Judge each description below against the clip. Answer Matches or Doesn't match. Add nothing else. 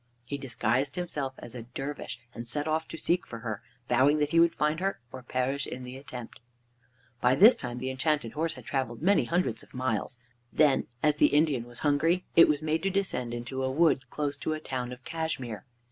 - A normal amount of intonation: Matches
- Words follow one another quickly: Matches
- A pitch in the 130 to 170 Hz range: Matches